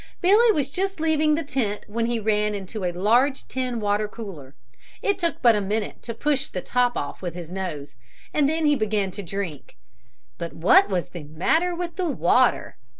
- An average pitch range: No, wide, 7.7 semitones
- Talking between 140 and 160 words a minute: No, average, 195 wpm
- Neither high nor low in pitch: No, high, 225 Hz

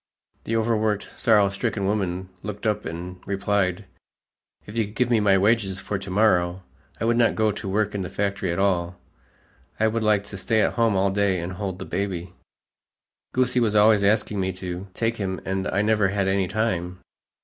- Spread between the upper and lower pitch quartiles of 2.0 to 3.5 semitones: Yes, narrow, 2.5 semitones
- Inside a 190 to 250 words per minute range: Yes, average, 195 wpm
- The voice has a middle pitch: No, low, 100 Hz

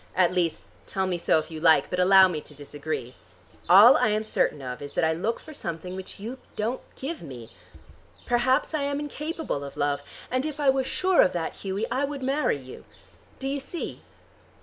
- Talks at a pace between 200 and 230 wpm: Yes, fast, 205 wpm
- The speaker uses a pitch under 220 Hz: Yes, high, 190 Hz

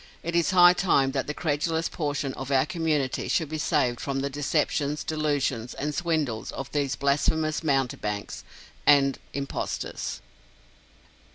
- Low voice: No, medium, 145 Hz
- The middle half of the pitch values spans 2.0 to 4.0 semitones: Yes, narrow, 2.6 semitones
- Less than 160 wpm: Yes, slow, 135 wpm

